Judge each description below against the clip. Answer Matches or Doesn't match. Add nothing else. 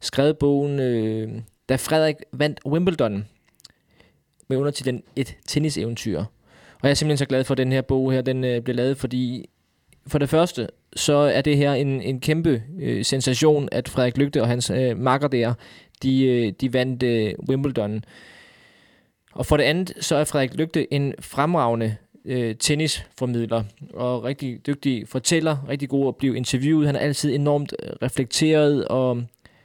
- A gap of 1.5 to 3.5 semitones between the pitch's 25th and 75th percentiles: Matches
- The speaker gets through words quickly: Doesn't match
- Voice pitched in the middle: Doesn't match